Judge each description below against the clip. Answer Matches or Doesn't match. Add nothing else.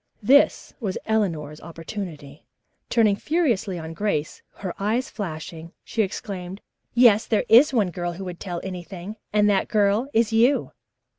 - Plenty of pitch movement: Doesn't match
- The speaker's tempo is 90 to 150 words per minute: Matches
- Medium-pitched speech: Doesn't match